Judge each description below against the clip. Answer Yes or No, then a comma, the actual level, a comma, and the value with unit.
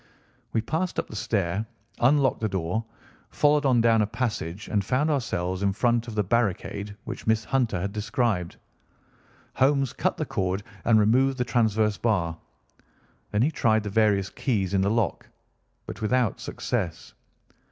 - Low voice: Yes, low, 110 Hz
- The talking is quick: No, average, 160 wpm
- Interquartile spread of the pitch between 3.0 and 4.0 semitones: Yes, average, 3.6 semitones